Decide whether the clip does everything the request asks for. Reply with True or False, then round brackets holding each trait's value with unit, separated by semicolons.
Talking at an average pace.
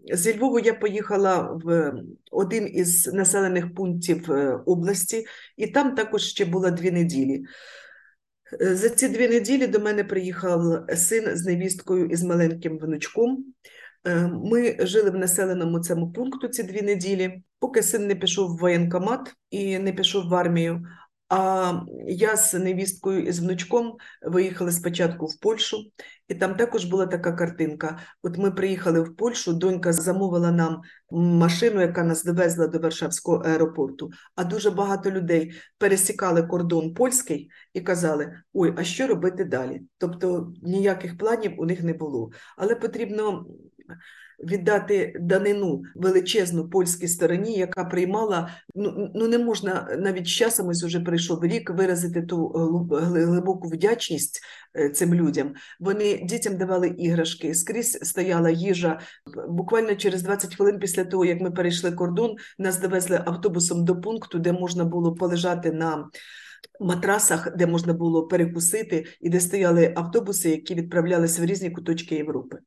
True (140 wpm)